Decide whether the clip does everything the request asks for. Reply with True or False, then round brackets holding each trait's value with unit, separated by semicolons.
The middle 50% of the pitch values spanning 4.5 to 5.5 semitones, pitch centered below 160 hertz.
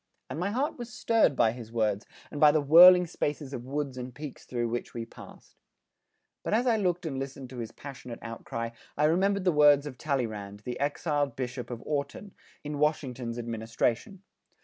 True (5.1 semitones; 140 Hz)